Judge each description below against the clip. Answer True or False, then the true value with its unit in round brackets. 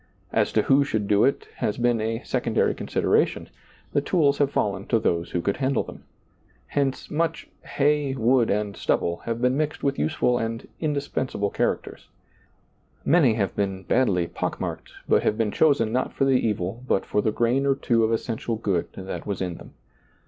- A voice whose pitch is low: True (115 Hz)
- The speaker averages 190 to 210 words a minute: True (195 wpm)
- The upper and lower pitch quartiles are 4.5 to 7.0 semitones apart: True (4.9 semitones)